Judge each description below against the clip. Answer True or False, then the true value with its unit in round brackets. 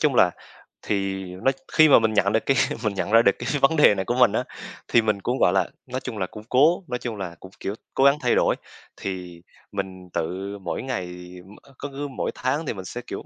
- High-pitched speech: False (105 Hz)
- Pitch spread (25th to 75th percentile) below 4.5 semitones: False (5.0 semitones)